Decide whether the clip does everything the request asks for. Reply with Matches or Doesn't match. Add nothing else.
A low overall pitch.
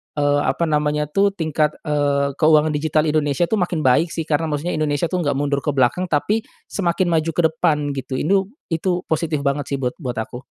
Doesn't match